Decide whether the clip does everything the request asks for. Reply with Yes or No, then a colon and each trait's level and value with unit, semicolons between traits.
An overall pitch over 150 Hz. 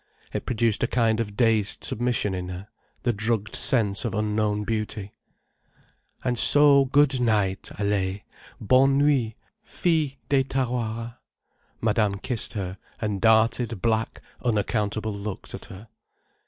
No: low, 110 Hz